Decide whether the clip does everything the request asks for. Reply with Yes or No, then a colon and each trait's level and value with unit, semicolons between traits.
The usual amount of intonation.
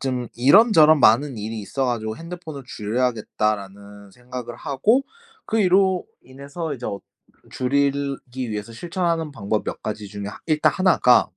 No: wide, 6.4 semitones